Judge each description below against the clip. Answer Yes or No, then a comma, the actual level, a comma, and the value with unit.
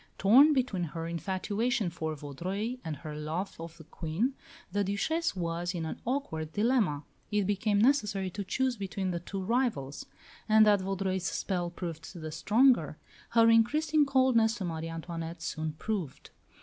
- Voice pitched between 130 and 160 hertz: No, high, 190 Hz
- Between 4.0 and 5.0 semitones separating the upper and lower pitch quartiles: No, wide, 5.5 semitones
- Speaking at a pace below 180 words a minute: Yes, average, 155 wpm